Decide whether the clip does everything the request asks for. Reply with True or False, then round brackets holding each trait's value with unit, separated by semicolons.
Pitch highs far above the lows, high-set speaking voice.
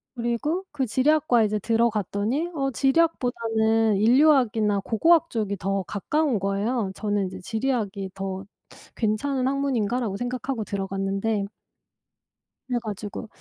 False (4.5 semitones; 225 Hz)